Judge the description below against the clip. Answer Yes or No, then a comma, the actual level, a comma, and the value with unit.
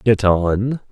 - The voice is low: Yes, low, 105 Hz